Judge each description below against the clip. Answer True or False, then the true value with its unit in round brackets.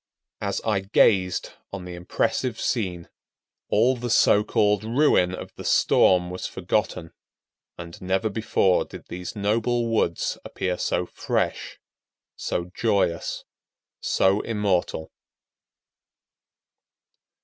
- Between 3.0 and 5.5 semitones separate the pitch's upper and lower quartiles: True (3.7 semitones)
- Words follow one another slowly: True (105 wpm)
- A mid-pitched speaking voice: False (100 Hz)